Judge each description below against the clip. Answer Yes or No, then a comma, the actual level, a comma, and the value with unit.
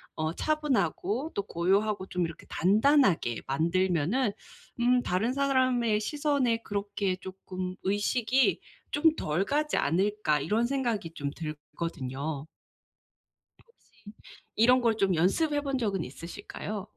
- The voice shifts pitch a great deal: Yes, wide, 6.5 semitones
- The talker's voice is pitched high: Yes, high, 205 Hz